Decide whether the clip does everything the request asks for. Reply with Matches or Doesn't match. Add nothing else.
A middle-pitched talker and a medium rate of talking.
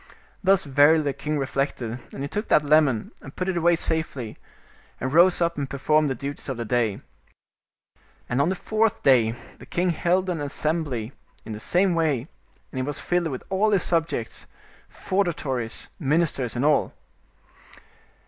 Matches